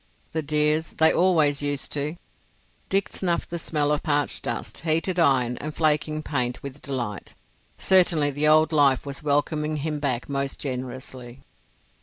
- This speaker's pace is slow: No, average, 145 wpm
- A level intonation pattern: Yes, narrow, 2.2 semitones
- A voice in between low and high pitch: Yes, medium, 150 Hz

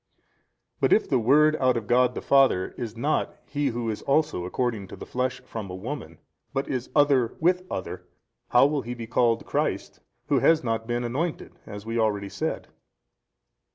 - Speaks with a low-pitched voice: Yes, low, 125 Hz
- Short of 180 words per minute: No, average, 190 wpm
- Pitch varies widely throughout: No, average, 3.8 semitones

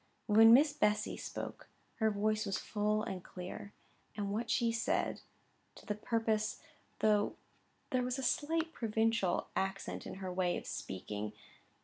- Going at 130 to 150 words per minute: Yes, average, 145 wpm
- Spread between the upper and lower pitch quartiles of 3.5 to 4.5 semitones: No, average, 2.7 semitones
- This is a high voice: Yes, high, 215 Hz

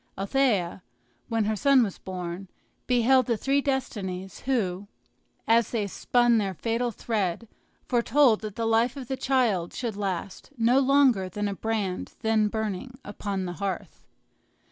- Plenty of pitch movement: No, average, 4.2 semitones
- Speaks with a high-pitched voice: Yes, high, 220 Hz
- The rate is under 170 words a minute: Yes, average, 145 wpm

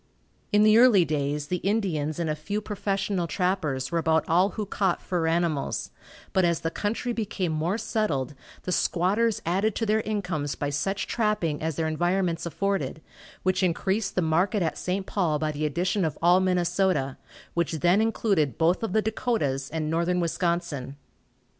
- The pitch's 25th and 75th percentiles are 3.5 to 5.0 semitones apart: Yes, average, 4.1 semitones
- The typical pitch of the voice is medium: Yes, medium, 175 Hz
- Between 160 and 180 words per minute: Yes, average, 170 wpm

